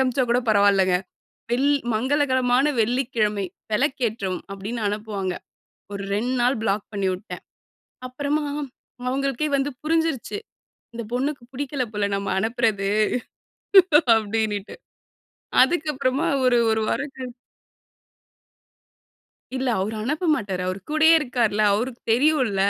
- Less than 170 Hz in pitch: No, high, 240 Hz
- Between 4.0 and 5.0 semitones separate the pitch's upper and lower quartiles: Yes, average, 4.6 semitones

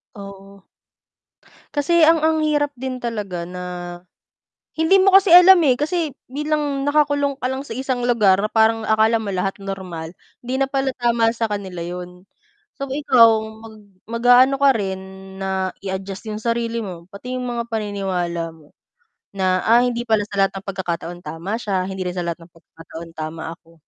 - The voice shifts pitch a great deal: Yes, wide, 5.7 semitones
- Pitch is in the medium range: No, high, 220 Hz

